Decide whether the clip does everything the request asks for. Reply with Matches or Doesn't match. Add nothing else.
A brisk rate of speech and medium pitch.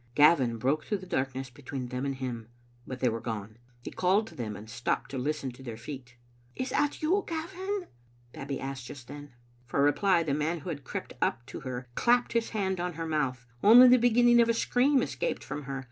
Matches